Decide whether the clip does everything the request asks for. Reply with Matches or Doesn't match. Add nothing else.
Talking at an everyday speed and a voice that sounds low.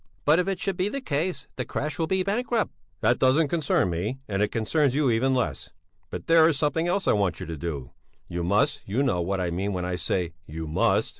Doesn't match